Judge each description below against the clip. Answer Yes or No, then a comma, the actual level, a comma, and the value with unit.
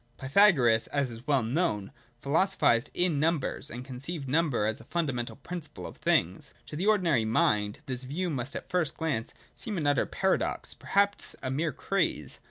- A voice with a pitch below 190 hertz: Yes, medium, 140 Hz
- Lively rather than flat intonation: Yes, wide, 6.0 semitones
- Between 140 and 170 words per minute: No, average, 180 wpm